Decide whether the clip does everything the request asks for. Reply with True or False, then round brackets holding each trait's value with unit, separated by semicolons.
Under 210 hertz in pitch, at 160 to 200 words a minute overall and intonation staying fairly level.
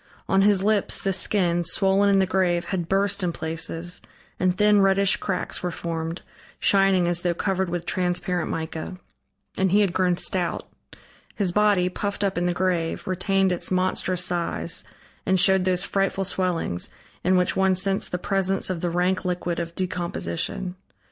True (185 Hz; 170 wpm; 1.7 semitones)